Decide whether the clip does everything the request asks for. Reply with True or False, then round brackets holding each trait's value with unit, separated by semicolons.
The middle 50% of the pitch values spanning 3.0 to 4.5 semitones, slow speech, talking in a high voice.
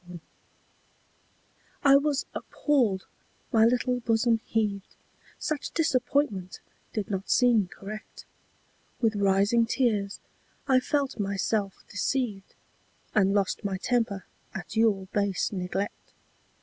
True (4.0 semitones; 110 wpm; 215 Hz)